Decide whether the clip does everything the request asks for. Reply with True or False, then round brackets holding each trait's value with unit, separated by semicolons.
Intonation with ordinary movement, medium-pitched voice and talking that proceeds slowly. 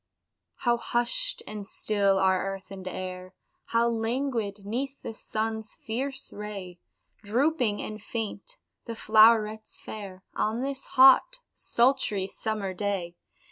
False (3.3 semitones; 215 Hz; 120 wpm)